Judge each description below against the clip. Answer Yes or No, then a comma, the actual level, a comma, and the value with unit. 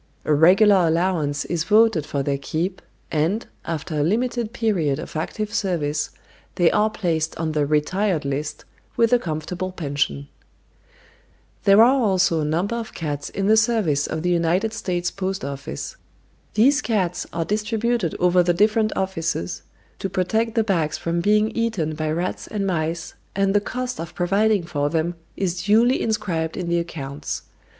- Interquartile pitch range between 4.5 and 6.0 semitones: Yes, average, 5.1 semitones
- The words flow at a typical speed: Yes, average, 160 wpm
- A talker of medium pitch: Yes, medium, 180 Hz